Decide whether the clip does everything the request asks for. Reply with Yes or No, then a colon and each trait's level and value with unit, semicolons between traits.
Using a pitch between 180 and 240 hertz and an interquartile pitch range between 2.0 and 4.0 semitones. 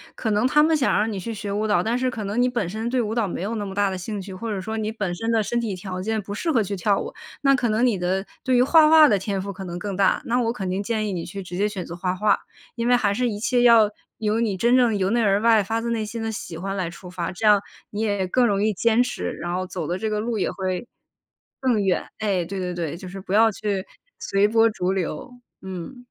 Yes: high, 210 Hz; average, 3.3 semitones